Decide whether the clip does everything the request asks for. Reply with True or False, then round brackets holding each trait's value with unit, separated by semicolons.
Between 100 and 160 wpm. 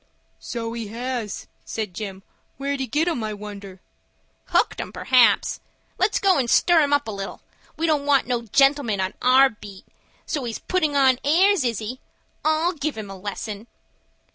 False (170 wpm)